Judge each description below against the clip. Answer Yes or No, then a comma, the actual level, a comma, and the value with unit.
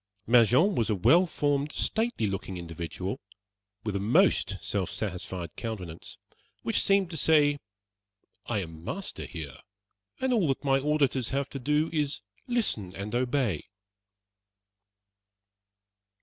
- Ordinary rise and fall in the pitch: No, wide, 7.7 semitones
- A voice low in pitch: Yes, low, 125 Hz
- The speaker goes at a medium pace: No, slow, 130 wpm